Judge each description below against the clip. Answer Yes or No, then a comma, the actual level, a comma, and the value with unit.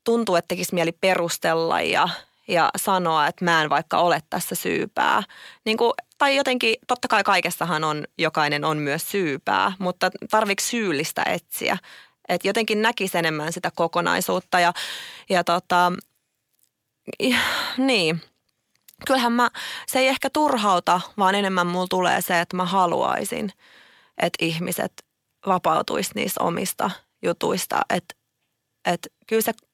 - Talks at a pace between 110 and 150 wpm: Yes, average, 130 wpm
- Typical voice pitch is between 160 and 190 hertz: Yes, medium, 185 Hz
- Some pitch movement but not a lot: Yes, average, 4.7 semitones